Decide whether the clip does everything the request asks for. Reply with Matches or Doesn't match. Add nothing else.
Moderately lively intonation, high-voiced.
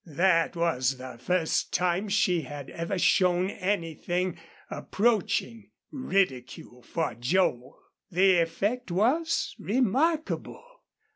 Doesn't match